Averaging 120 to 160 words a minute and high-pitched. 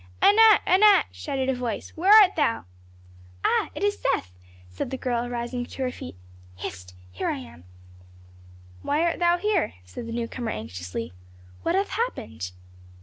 Yes: average, 155 wpm; high, 245 Hz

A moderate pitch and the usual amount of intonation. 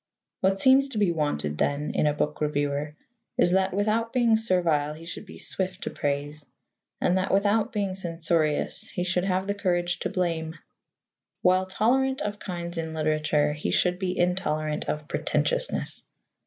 Yes: medium, 180 Hz; average, 4.4 semitones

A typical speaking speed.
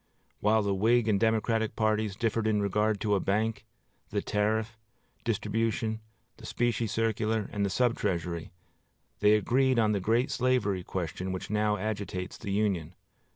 Yes: average, 155 wpm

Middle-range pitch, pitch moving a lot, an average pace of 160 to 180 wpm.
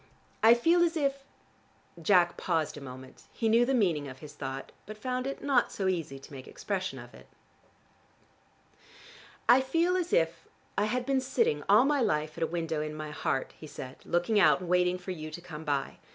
No: medium, 180 Hz; wide, 8.6 semitones; fast, 205 wpm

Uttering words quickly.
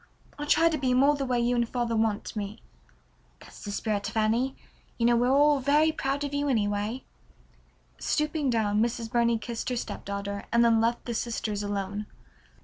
No: average, 185 wpm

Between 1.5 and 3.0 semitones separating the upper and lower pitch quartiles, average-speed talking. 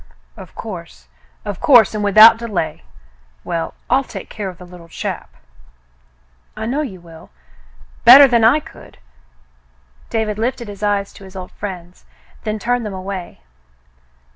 No: average, 3.7 semitones; average, 145 wpm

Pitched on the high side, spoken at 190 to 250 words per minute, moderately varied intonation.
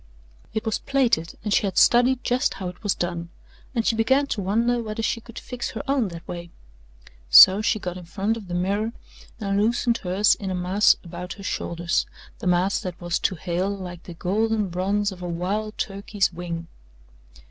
Yes: high, 195 Hz; average, 195 wpm; average, 3.8 semitones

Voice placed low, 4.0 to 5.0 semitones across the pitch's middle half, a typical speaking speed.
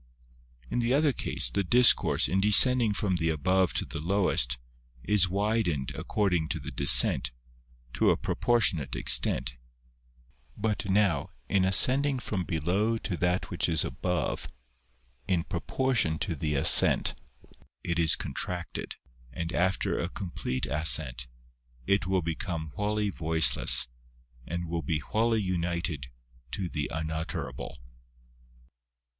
No: very low, 90 Hz; average, 4.3 semitones; slow, 125 wpm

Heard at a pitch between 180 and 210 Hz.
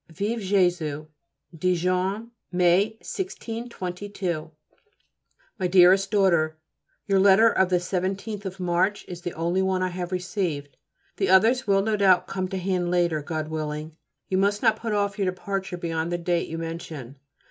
Yes: medium, 185 Hz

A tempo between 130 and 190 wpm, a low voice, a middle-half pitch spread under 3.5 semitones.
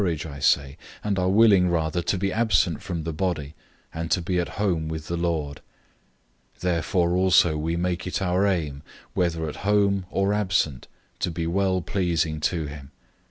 No: fast, 205 wpm; very low, 85 Hz; average, 2.9 semitones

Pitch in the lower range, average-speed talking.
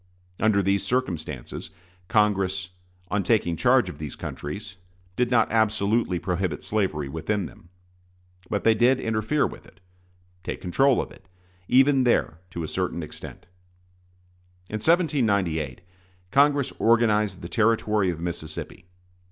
No: low, 100 Hz; slow, 125 wpm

